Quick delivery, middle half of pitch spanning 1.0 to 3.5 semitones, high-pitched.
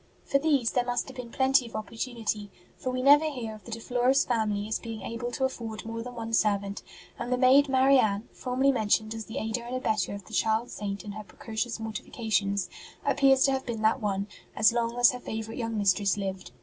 Yes: fast, 215 wpm; average, 2.8 semitones; high, 230 Hz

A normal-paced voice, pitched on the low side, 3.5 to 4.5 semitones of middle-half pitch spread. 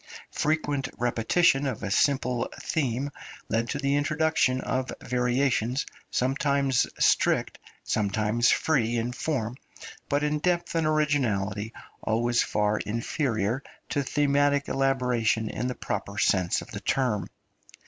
No: slow, 120 wpm; low, 130 Hz; average, 3.9 semitones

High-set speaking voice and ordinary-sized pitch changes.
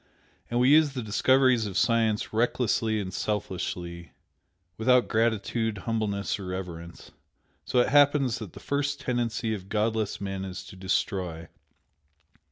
No: low, 110 Hz; average, 4.2 semitones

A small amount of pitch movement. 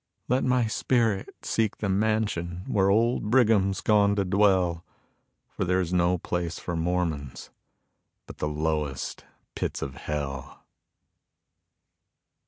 No: average, 4.2 semitones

